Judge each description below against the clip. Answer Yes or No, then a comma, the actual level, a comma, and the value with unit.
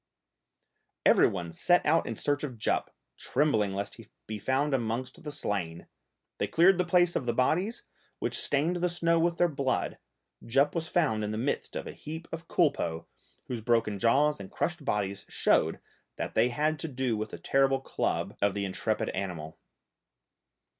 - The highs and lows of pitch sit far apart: Yes, wide, 7.1 semitones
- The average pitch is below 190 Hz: Yes, low, 135 Hz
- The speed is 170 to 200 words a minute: Yes, average, 180 wpm